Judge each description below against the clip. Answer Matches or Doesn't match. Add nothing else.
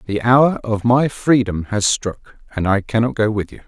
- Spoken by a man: Matches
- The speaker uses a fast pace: Matches